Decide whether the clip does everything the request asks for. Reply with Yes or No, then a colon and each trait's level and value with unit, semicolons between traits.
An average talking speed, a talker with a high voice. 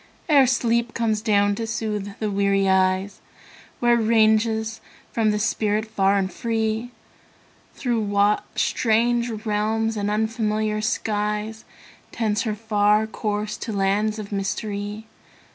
No: slow, 125 wpm; high, 215 Hz